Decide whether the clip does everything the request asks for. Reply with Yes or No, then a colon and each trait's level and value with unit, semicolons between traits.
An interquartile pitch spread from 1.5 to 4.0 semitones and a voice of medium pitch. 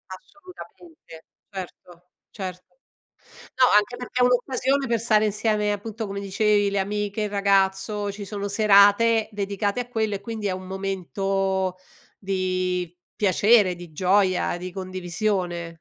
No: narrow, 2.4 semitones; high, 200 Hz